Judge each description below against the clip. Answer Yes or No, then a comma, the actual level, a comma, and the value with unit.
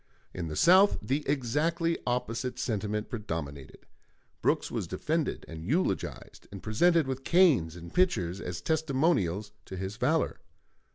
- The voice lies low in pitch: Yes, low, 120 Hz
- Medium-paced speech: No, slow, 130 wpm